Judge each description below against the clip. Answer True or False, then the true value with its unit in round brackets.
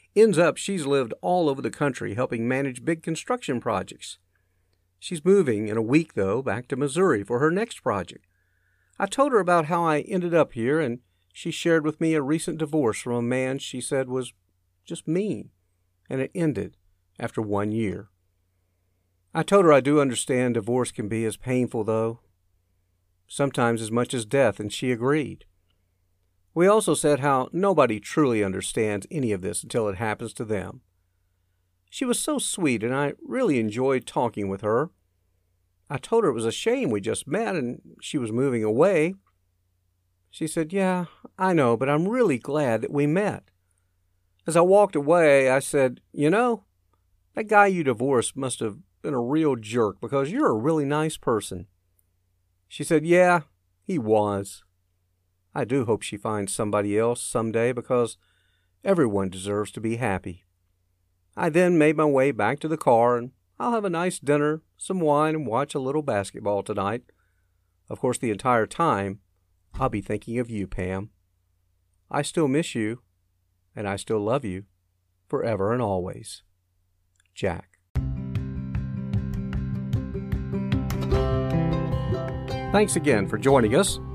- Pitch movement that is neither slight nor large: False (8.1 semitones)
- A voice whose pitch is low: True (115 Hz)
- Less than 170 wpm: True (160 wpm)